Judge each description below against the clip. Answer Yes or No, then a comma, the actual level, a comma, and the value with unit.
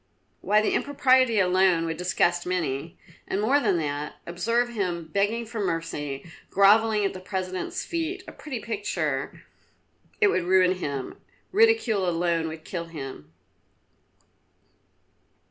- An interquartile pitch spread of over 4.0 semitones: Yes, average, 5.3 semitones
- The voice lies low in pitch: No, medium, 185 Hz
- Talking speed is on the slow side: Yes, slow, 130 wpm